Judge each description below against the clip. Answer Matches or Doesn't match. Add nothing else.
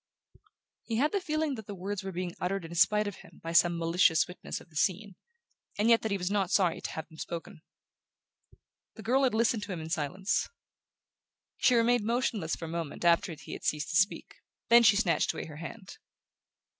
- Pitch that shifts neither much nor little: Matches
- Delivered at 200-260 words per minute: Matches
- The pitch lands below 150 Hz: Doesn't match